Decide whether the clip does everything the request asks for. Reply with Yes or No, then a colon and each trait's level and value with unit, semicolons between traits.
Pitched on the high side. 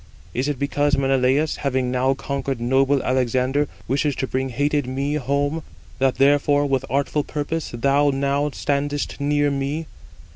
No: medium, 140 Hz